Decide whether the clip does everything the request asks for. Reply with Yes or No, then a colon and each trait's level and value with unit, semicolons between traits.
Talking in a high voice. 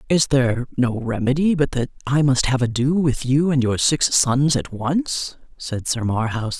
No: low, 135 Hz